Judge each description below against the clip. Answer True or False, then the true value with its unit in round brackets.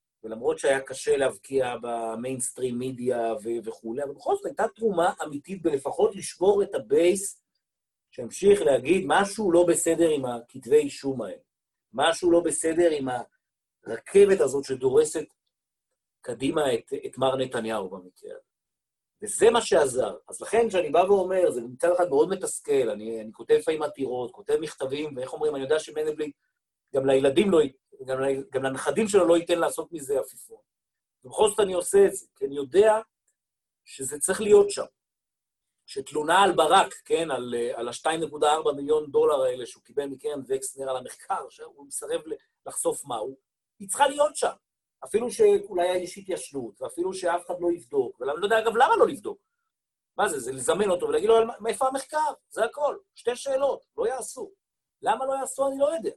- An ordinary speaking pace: False (160 wpm)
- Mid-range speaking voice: False (210 Hz)